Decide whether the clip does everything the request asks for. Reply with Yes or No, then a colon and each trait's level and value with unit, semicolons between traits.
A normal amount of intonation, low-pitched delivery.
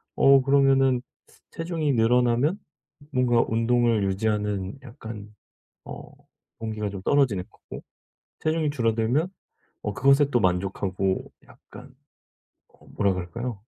Yes: average, 4.8 semitones; low, 115 Hz